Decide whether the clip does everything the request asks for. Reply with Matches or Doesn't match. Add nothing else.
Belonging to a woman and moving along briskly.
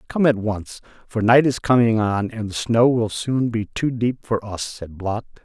Doesn't match